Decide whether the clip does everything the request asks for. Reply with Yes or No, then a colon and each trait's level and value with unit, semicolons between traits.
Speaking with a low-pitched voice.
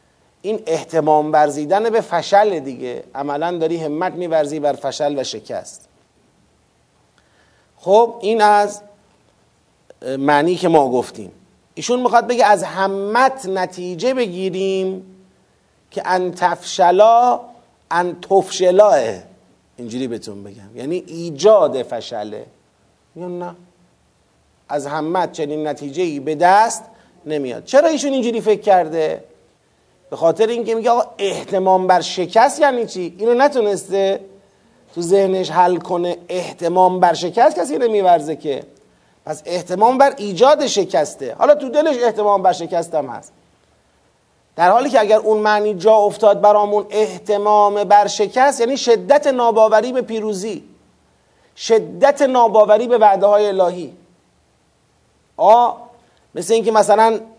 No: high, 195 Hz